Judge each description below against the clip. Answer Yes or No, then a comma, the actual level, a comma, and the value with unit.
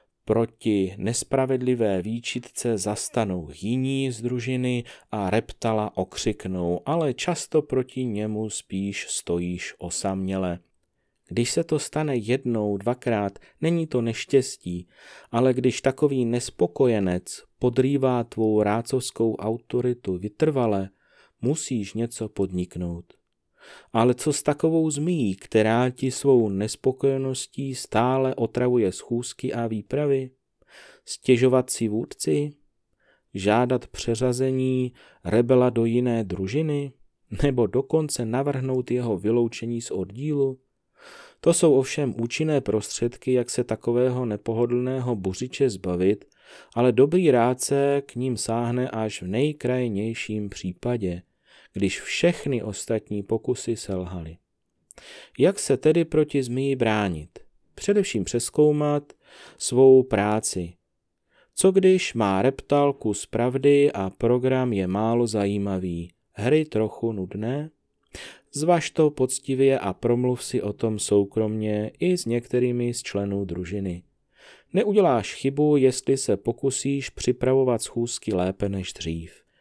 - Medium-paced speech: No, slow, 110 wpm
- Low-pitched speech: Yes, low, 120 Hz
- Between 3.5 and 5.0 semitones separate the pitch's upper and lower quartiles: Yes, average, 4.0 semitones